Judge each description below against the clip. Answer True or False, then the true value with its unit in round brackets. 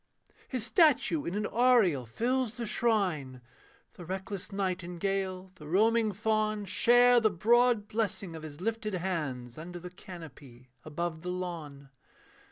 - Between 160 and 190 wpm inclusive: False (135 wpm)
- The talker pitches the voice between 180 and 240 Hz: True (190 Hz)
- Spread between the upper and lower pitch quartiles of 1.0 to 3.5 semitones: False (4.8 semitones)